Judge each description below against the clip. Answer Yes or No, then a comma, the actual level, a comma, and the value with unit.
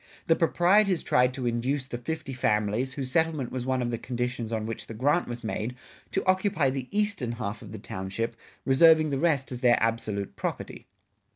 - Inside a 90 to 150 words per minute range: No, average, 190 wpm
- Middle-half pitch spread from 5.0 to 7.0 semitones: Yes, average, 5.3 semitones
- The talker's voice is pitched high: No, low, 125 Hz